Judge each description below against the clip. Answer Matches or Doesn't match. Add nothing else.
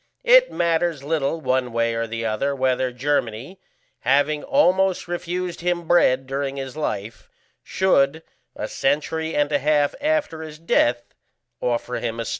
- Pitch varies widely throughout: Doesn't match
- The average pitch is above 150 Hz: Doesn't match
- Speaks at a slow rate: Doesn't match